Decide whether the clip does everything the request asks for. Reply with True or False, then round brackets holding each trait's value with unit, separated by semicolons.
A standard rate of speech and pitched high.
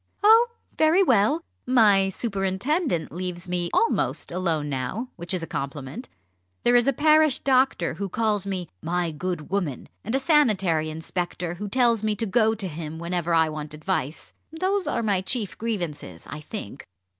True (165 wpm; 195 Hz)